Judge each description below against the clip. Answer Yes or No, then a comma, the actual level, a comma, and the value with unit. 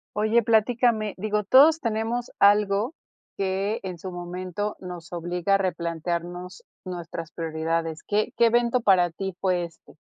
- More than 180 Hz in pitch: Yes, high, 190 Hz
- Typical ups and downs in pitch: Yes, average, 3.7 semitones